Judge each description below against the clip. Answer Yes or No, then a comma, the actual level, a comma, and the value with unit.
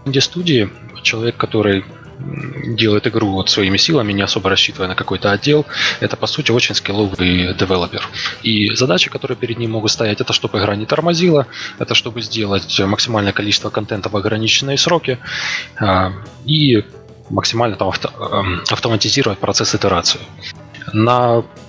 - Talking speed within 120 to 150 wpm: Yes, average, 140 wpm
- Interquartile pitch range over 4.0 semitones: No, average, 3.4 semitones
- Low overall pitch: Yes, low, 110 Hz